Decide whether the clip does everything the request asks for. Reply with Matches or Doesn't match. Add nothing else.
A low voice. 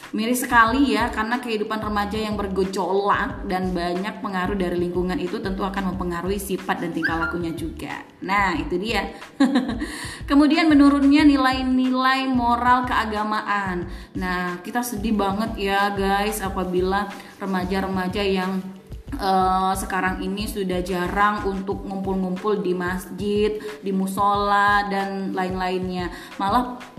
Doesn't match